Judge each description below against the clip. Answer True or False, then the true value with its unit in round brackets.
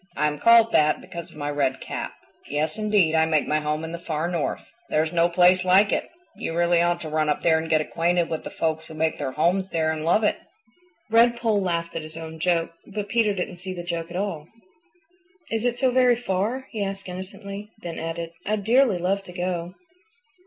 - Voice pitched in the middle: True (175 Hz)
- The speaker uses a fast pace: True (220 wpm)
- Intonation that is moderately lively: True (3.8 semitones)